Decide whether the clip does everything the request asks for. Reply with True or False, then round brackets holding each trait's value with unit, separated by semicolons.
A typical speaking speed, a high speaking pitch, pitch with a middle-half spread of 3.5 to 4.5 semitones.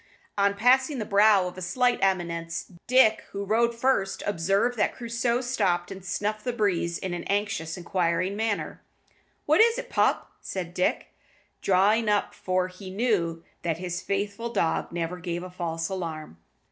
True (160 wpm; 195 Hz; 4.1 semitones)